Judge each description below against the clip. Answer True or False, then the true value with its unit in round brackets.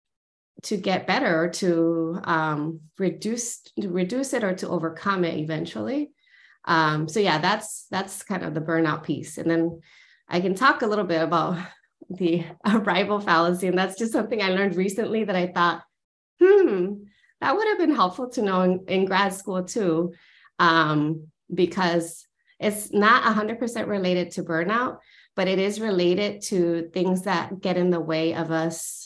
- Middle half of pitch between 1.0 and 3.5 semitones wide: False (3.9 semitones)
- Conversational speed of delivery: True (165 wpm)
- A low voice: False (185 Hz)